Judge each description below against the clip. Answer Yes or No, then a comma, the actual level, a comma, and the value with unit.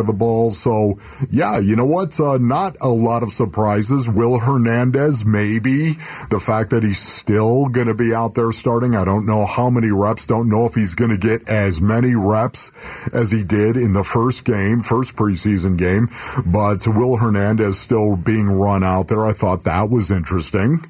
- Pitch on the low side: Yes, low, 110 Hz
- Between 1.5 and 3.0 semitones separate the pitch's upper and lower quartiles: Yes, narrow, 2.6 semitones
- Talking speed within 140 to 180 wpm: No, average, 195 wpm